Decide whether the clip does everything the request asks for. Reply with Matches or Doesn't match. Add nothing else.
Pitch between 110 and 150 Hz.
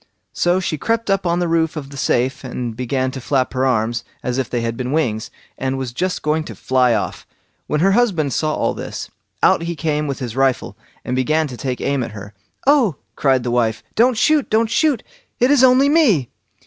Matches